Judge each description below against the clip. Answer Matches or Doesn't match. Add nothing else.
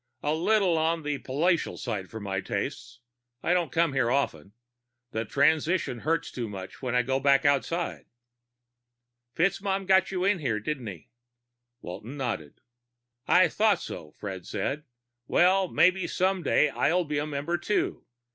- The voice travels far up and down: Matches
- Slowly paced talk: Doesn't match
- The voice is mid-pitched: Matches